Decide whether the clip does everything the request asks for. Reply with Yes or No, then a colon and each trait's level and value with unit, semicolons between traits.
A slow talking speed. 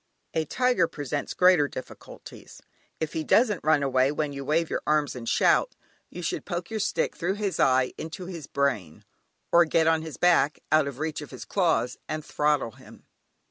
No: average, 185 wpm